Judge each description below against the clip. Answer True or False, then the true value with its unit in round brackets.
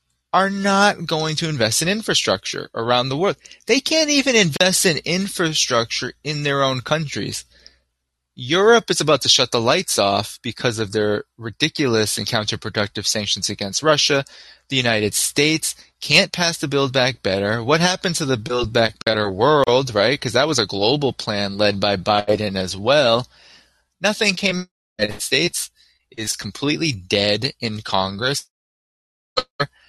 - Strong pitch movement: True (7.6 semitones)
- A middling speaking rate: True (160 wpm)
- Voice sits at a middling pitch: False (125 Hz)